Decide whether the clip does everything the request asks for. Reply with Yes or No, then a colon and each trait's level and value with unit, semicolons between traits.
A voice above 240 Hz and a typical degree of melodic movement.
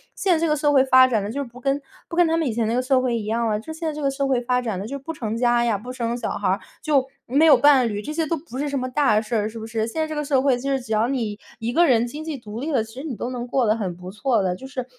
Yes: very high, 250 Hz; average, 4.0 semitones